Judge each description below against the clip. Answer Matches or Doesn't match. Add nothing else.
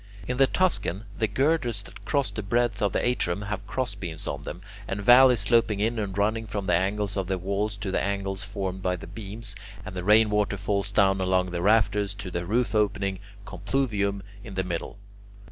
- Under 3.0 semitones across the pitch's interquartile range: Matches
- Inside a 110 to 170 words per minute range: Doesn't match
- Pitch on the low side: Matches